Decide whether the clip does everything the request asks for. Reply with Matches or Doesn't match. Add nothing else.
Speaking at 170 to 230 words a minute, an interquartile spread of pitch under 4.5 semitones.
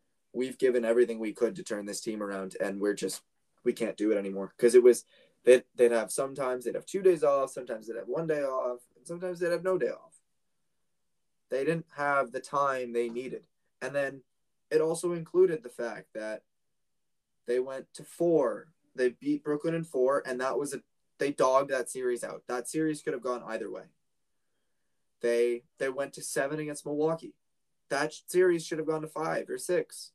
Doesn't match